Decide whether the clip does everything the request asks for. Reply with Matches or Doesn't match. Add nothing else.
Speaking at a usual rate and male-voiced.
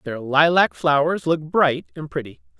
Matches